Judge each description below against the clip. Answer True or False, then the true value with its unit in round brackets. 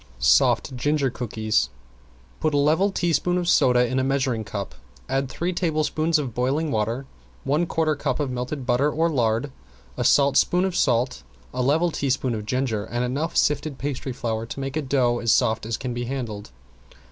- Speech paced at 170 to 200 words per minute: True (180 wpm)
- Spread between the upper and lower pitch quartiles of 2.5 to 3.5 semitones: False (3.9 semitones)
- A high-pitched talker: False (135 Hz)